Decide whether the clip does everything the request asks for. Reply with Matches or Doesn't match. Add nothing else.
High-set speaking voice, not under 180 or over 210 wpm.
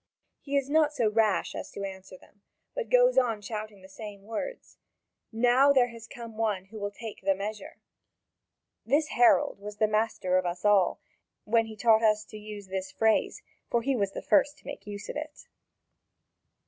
Matches